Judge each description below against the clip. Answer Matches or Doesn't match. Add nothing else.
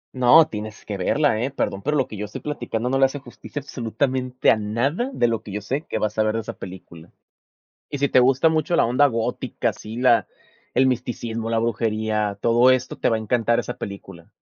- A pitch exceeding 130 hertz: Doesn't match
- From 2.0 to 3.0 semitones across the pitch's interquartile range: Doesn't match